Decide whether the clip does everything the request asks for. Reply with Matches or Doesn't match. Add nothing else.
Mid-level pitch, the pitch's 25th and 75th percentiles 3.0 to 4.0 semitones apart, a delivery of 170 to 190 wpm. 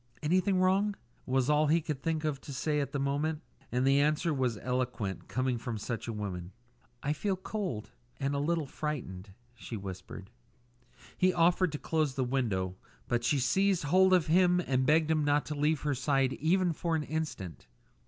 Doesn't match